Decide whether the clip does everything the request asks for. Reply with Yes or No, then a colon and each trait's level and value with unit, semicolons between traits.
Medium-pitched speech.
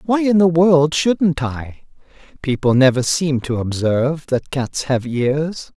Yes: medium, 145 Hz